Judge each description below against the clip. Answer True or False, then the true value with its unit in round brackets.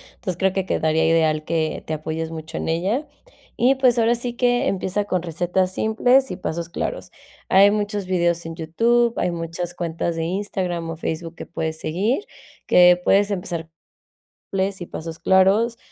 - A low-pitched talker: False (180 Hz)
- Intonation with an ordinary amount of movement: True (4.0 semitones)